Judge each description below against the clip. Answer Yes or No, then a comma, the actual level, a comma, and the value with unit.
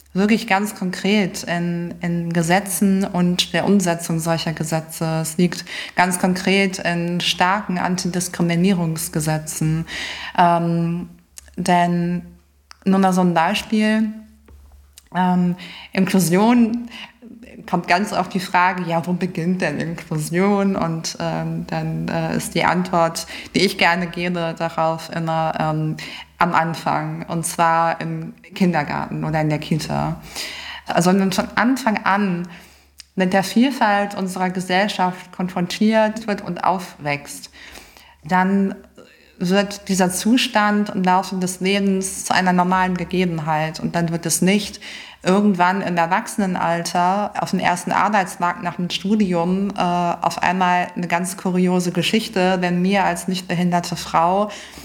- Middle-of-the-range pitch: Yes, medium, 180 Hz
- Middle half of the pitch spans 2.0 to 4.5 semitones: Yes, narrow, 2.4 semitones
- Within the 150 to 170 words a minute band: No, slow, 125 wpm